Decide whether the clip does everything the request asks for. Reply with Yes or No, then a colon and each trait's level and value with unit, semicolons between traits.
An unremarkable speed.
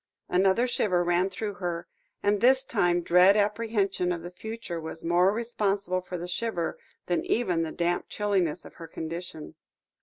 Yes: average, 160 wpm